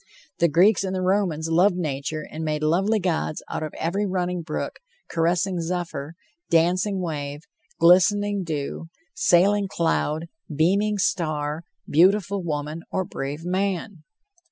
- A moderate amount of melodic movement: Yes, average, 3.4 semitones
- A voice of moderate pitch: Yes, medium, 170 Hz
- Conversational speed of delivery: No, slow, 130 wpm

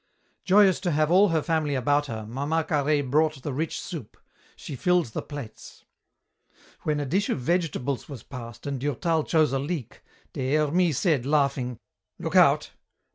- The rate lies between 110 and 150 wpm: No, average, 165 wpm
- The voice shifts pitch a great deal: No, average, 3.3 semitones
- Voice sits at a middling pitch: Yes, medium, 145 Hz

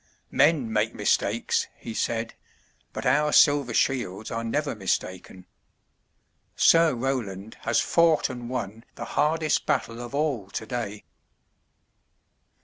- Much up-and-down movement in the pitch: No, average, 4.7 semitones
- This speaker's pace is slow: Yes, slow, 115 wpm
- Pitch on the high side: No, low, 120 Hz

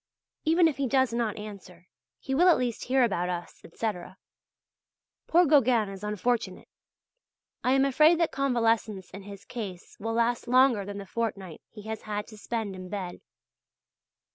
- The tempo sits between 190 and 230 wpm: No, average, 165 wpm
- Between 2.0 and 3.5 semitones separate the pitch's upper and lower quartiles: No, average, 4.5 semitones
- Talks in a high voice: Yes, high, 225 Hz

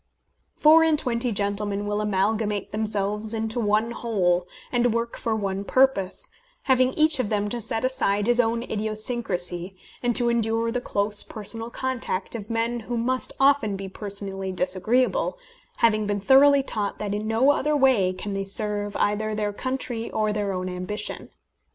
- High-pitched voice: Yes, high, 215 Hz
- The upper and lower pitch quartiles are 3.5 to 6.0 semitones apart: No, average, 3.0 semitones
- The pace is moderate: Yes, average, 165 wpm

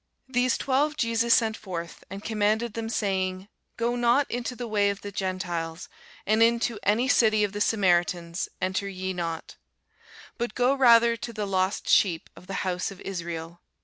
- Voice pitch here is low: No, high, 205 Hz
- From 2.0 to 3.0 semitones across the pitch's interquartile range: No, average, 4.0 semitones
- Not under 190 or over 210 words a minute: No, average, 170 wpm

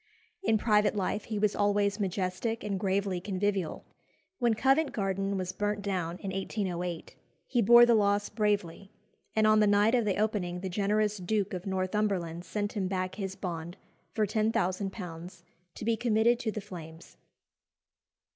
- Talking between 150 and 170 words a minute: Yes, average, 155 wpm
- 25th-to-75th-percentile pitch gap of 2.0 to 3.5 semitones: Yes, narrow, 2.5 semitones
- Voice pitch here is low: No, high, 200 Hz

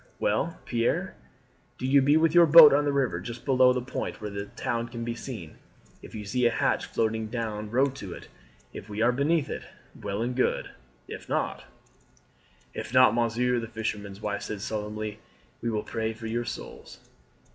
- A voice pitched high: No, low, 115 Hz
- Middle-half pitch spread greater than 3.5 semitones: No, average, 3.2 semitones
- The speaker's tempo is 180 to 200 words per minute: Yes, average, 190 wpm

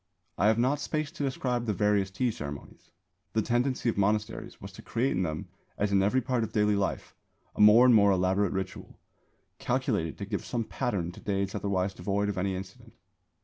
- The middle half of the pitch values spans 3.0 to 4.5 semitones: Yes, average, 3.8 semitones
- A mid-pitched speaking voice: No, low, 105 Hz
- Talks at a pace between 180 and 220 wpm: Yes, average, 195 wpm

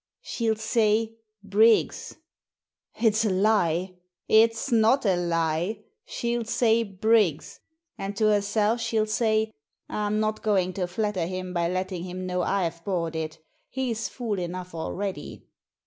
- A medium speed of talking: No, slow, 130 wpm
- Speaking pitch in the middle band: No, high, 205 Hz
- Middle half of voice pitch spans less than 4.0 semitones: Yes, average, 3.4 semitones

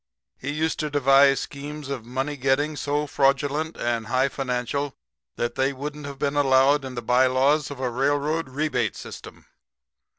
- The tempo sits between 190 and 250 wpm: No, average, 160 wpm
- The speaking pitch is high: No, medium, 140 Hz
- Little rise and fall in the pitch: Yes, narrow, 2.0 semitones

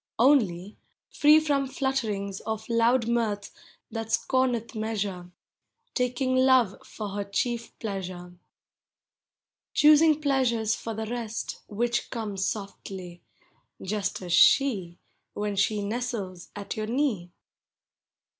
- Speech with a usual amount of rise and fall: Yes, average, 4.0 semitones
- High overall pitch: Yes, high, 220 Hz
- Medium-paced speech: No, slow, 110 wpm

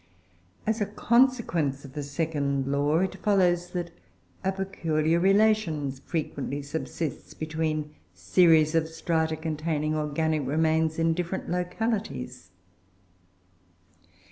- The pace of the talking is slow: Yes, slow, 105 wpm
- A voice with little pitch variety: No, average, 3.1 semitones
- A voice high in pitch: No, medium, 160 Hz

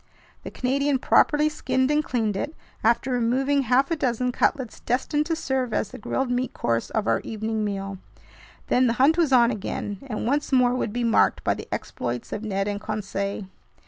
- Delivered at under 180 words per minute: No, average, 190 wpm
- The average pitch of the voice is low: No, high, 245 Hz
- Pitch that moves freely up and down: No, average, 4.0 semitones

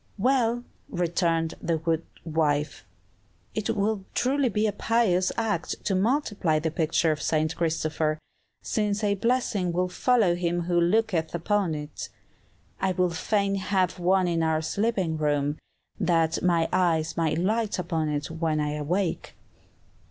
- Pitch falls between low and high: Yes, medium, 175 Hz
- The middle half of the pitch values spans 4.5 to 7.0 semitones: No, average, 4.1 semitones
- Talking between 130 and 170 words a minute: Yes, average, 145 wpm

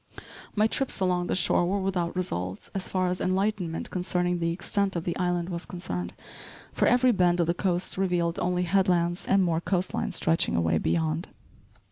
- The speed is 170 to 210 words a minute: Yes, average, 180 wpm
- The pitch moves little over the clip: Yes, narrow, 1.8 semitones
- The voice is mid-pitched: Yes, medium, 180 Hz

